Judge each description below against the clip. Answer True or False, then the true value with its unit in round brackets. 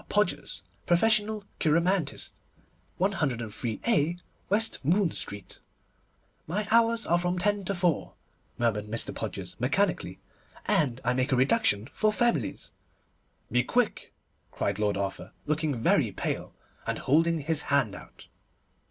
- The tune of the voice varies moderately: False (8.4 semitones)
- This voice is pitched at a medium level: True (160 Hz)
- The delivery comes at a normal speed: False (120 wpm)